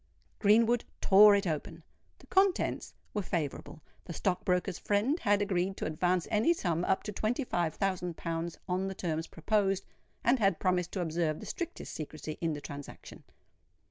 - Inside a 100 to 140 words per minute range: No, average, 170 wpm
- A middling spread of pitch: Yes, average, 3.9 semitones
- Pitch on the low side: No, medium, 185 Hz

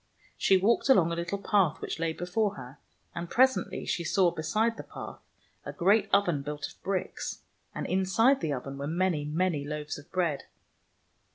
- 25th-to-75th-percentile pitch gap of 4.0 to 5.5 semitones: Yes, average, 4.7 semitones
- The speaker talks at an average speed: Yes, average, 175 wpm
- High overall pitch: No, medium, 175 Hz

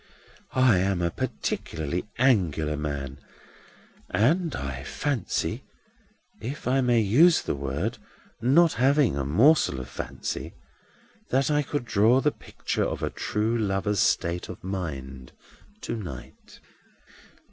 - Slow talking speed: Yes, slow, 125 wpm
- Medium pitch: No, low, 105 Hz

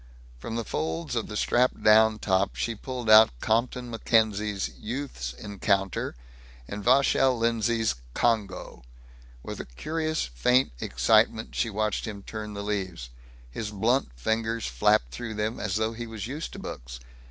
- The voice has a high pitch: No, low, 110 Hz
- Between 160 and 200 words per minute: No, average, 150 wpm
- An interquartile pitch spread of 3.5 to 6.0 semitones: No, average, 2.9 semitones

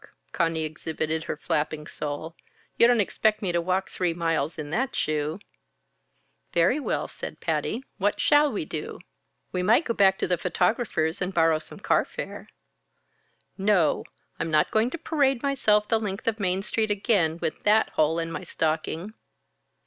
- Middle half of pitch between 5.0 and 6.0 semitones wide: Yes, average, 5.3 semitones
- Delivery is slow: No, average, 165 wpm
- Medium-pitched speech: Yes, medium, 180 Hz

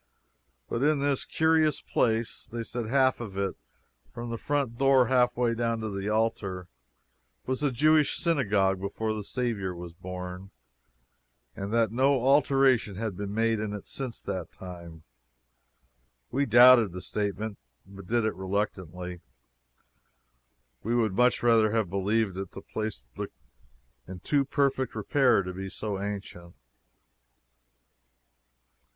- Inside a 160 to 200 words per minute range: No, average, 140 wpm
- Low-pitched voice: Yes, low, 110 Hz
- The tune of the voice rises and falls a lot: No, average, 4.5 semitones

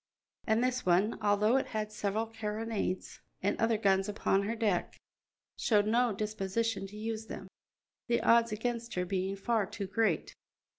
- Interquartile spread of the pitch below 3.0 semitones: Yes, narrow, 2.5 semitones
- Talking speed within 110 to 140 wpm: No, average, 155 wpm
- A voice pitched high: Yes, high, 215 Hz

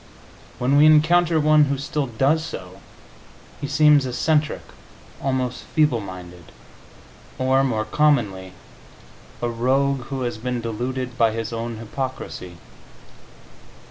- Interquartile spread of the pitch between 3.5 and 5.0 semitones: Yes, average, 4.2 semitones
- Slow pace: Yes, slow, 115 wpm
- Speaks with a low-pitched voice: Yes, low, 130 Hz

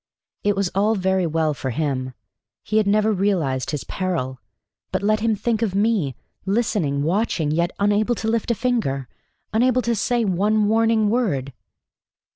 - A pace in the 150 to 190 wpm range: Yes, average, 160 wpm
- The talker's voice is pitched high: Yes, high, 200 Hz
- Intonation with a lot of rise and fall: Yes, wide, 5.7 semitones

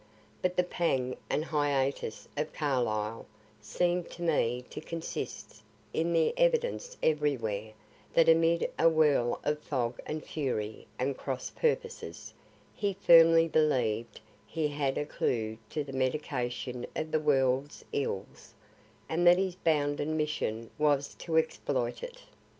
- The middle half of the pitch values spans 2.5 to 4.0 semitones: No, average, 4.5 semitones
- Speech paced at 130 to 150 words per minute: Yes, slow, 135 wpm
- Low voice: No, medium, 150 Hz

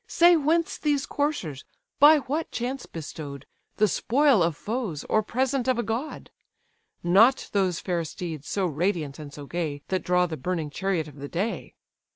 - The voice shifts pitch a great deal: Yes, wide, 8.6 semitones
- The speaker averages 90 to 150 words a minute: No, average, 170 wpm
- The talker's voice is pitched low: No, high, 190 Hz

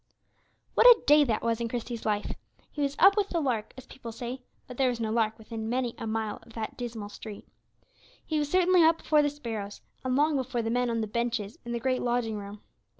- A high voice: Yes, high, 240 Hz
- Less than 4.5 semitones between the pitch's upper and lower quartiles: Yes, average, 3.8 semitones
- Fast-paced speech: Yes, fast, 230 wpm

